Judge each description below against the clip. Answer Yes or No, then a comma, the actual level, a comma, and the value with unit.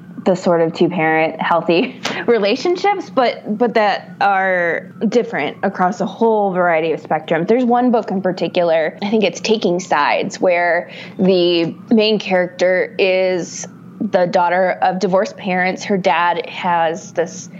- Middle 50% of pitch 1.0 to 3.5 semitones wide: Yes, average, 3.0 semitones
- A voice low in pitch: No, medium, 185 Hz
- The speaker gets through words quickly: No, average, 145 wpm